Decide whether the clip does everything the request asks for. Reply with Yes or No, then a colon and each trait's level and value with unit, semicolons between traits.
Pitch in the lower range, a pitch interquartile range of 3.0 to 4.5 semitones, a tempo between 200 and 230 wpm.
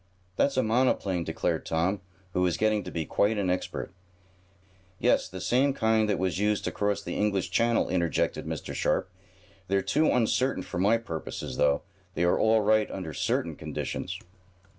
No: low, 105 Hz; average, 3.6 semitones; average, 170 wpm